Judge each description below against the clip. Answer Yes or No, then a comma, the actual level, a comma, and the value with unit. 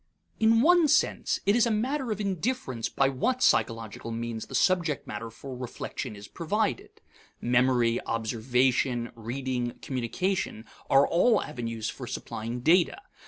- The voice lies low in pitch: Yes, low, 130 Hz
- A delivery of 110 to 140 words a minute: Yes, slow, 135 wpm